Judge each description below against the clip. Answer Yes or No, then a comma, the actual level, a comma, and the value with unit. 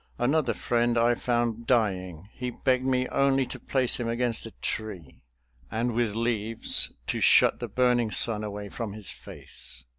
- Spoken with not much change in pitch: Yes, narrow, 2.3 semitones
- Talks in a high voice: No, low, 115 Hz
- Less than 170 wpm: Yes, average, 160 wpm